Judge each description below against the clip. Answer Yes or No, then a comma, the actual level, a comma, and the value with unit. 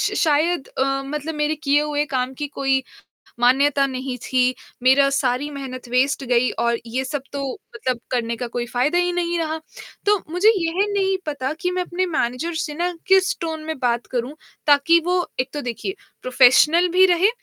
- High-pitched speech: Yes, very high, 285 Hz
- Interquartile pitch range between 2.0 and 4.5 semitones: No, average, 4.9 semitones